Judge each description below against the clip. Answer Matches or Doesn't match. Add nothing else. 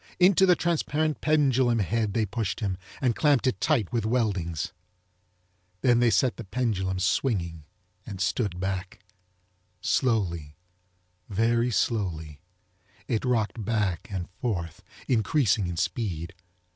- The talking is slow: Matches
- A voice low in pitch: Matches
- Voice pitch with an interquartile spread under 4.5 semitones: Doesn't match